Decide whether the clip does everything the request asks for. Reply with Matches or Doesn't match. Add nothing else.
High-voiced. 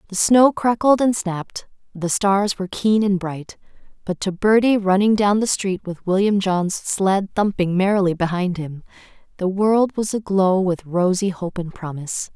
Matches